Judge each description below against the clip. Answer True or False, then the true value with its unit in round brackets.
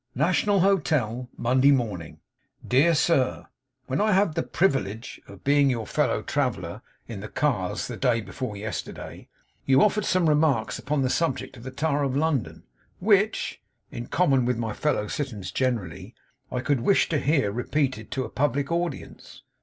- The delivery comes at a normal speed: True (160 wpm)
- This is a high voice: False (135 Hz)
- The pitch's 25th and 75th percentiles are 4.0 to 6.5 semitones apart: True (5.1 semitones)